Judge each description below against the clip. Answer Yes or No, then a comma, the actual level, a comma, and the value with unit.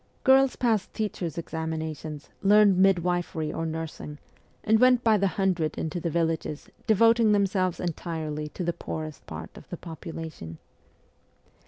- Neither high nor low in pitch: Yes, medium, 170 Hz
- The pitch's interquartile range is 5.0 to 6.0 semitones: No, average, 4.3 semitones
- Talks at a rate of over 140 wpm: No, slow, 135 wpm